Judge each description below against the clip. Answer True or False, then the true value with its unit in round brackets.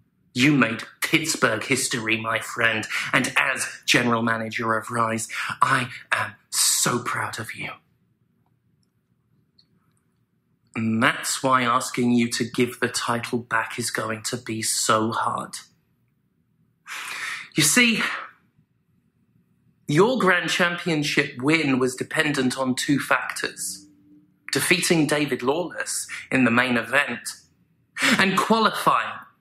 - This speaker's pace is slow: True (110 wpm)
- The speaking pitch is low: True (125 Hz)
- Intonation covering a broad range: False (4.5 semitones)